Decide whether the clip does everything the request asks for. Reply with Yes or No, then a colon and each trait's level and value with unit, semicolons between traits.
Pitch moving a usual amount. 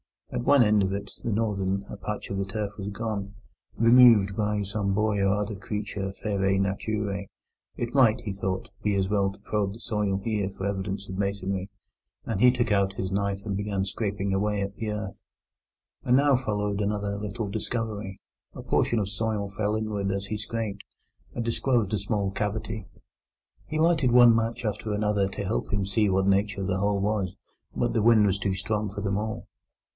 No: narrow, 1.8 semitones